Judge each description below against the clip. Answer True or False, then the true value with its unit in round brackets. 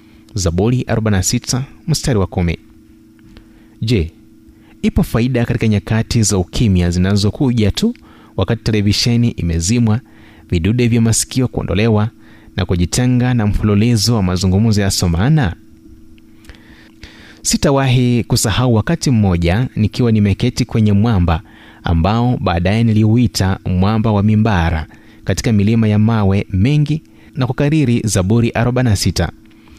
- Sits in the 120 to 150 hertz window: False (110 Hz)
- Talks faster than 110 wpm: False (105 wpm)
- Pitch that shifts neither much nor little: True (3.6 semitones)